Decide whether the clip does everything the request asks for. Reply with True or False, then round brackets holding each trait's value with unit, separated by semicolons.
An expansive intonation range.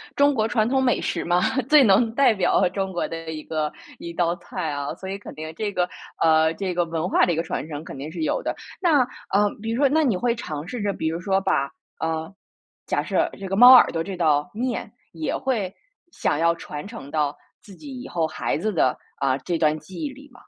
True (6.0 semitones)